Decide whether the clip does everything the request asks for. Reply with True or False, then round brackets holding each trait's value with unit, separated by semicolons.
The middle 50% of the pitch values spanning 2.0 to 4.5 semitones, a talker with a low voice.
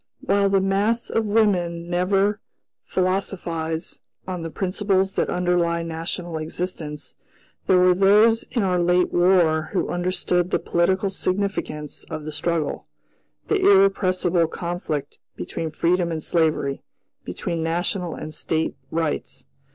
False (2.7 semitones; 180 Hz)